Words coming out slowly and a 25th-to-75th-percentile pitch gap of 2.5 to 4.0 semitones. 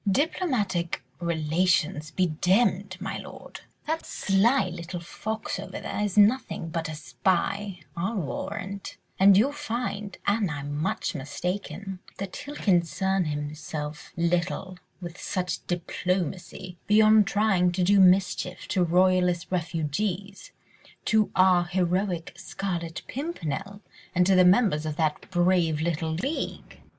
Yes: slow, 120 wpm; average, 2.9 semitones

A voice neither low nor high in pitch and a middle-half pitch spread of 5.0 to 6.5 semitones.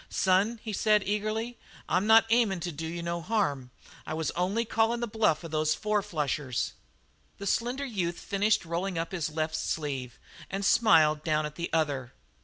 Yes: medium, 180 Hz; wide, 5.4 semitones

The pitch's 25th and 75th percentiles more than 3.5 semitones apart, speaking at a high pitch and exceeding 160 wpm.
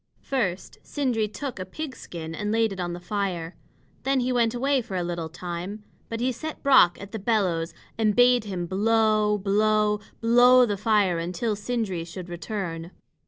Yes: average, 4.7 semitones; high, 210 Hz; average, 175 wpm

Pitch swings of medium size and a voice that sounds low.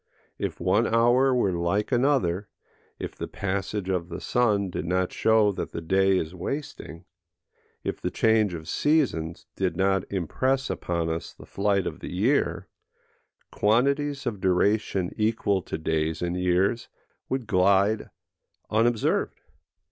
Yes: average, 4.3 semitones; low, 100 Hz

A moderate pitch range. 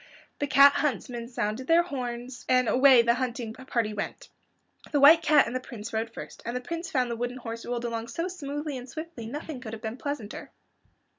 Yes: average, 3.4 semitones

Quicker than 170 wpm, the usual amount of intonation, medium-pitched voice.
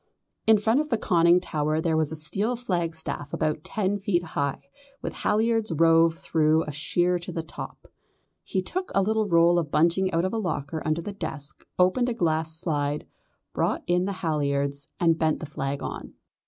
Yes: average, 185 wpm; average, 3.6 semitones; medium, 165 Hz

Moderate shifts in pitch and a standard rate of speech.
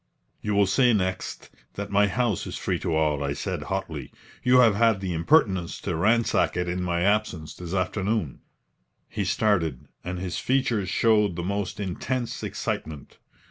Yes: average, 3.7 semitones; average, 165 wpm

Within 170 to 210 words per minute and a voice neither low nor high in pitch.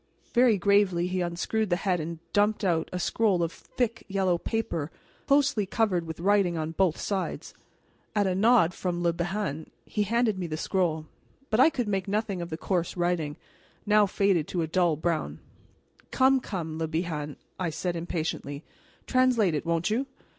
Yes: average, 175 wpm; medium, 180 Hz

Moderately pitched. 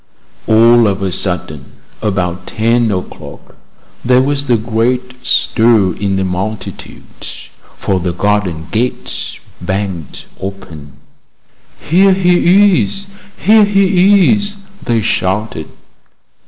No: low, 110 Hz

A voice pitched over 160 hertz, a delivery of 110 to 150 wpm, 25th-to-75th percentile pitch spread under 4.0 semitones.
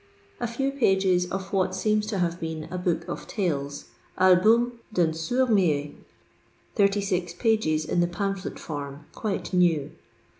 No: medium, 185 Hz; average, 145 wpm; average, 4.3 semitones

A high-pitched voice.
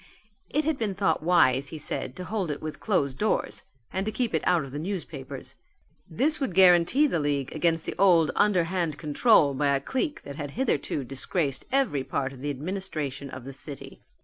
No: medium, 160 Hz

